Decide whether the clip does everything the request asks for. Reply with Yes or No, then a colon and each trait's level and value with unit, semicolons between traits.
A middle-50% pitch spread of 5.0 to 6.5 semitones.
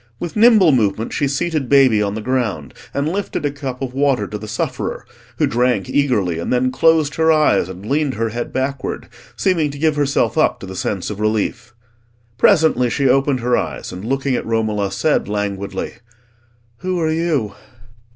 Yes: wide, 5.5 semitones